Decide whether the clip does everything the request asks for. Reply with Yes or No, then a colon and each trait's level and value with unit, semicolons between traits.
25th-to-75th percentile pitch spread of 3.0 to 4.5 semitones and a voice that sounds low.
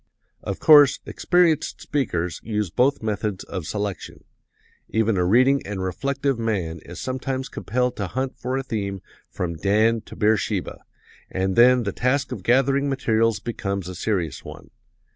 No: average, 5.1 semitones; low, 110 Hz